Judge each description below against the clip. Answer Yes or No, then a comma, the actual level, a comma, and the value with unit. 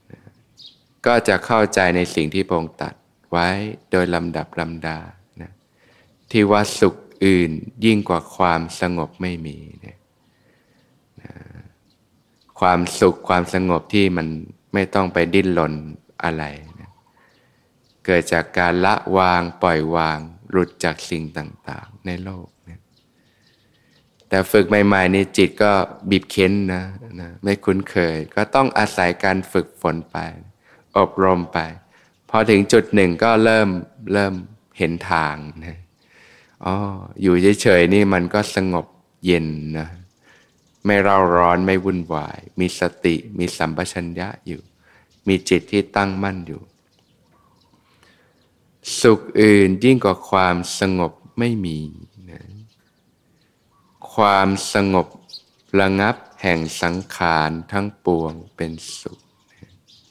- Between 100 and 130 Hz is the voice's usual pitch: No, very low, 90 Hz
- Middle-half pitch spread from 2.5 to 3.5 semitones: Yes, average, 2.8 semitones